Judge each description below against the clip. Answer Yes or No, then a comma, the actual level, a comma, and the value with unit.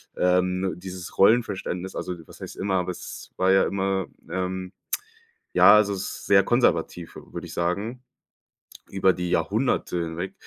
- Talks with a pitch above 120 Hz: No, very low, 95 Hz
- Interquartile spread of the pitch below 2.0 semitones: Yes, narrow, 1.5 semitones